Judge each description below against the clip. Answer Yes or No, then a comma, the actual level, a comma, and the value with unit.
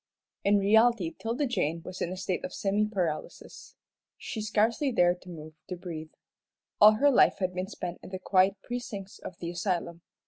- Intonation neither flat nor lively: Yes, average, 3.4 semitones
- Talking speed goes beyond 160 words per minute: Yes, average, 180 wpm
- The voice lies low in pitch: No, high, 190 Hz